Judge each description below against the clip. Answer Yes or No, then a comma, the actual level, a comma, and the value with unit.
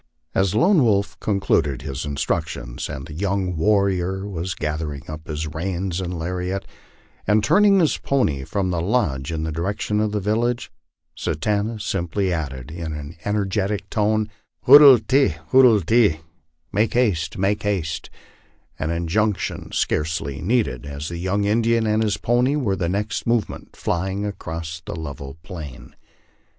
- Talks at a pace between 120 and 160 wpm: Yes, average, 155 wpm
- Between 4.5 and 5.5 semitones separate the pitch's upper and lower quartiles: Yes, average, 4.9 semitones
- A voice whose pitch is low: Yes, very low, 95 Hz